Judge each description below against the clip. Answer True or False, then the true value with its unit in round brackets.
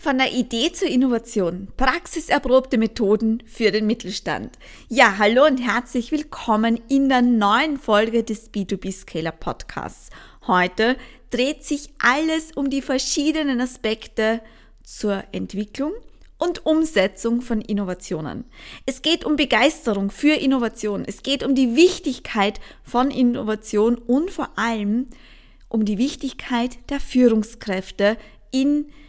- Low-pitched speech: False (245 Hz)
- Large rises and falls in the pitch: False (4.4 semitones)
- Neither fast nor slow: False (120 wpm)